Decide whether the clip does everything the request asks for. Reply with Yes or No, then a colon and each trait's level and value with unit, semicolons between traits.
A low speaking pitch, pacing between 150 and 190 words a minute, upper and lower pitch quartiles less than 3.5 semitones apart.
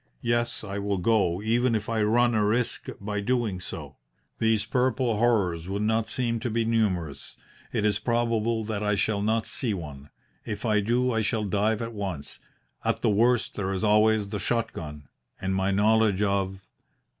Yes: low, 105 Hz; average, 180 wpm; narrow, 2.6 semitones